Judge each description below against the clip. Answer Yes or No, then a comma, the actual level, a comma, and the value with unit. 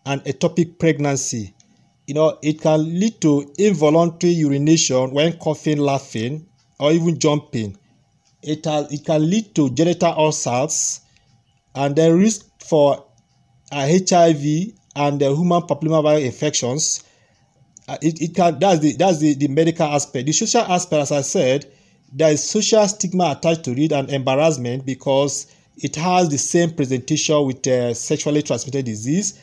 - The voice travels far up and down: No, average, 3.2 semitones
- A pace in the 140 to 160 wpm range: Yes, average, 150 wpm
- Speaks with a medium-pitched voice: Yes, medium, 150 Hz